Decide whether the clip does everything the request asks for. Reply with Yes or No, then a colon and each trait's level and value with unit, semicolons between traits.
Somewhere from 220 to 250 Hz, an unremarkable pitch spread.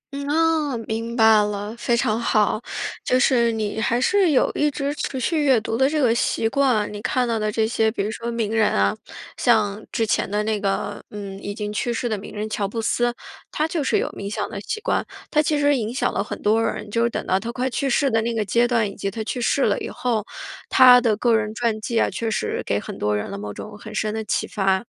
Yes: high, 225 Hz; average, 3.0 semitones